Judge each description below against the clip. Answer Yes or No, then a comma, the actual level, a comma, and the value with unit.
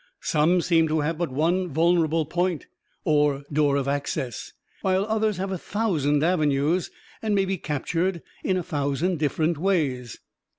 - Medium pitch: Yes, medium, 165 Hz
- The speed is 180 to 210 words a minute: No, average, 155 wpm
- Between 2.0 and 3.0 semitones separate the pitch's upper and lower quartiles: No, average, 3.9 semitones